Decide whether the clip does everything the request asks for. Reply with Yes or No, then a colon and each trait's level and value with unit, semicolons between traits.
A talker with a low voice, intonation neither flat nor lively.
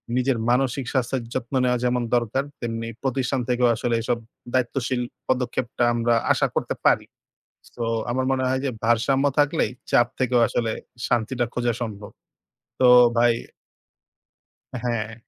No: low, 125 Hz; narrow, 1.7 semitones